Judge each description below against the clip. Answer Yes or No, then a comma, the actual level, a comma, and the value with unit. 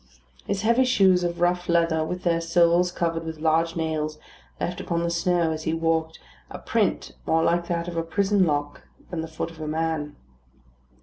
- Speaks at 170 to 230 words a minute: Yes, average, 190 wpm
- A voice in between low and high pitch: Yes, medium, 165 Hz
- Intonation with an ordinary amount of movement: No, narrow, 1.6 semitones